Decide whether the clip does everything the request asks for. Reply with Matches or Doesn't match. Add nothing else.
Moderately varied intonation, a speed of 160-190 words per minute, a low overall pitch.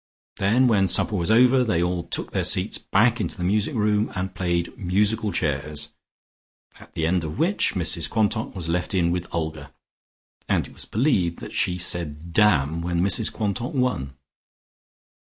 Matches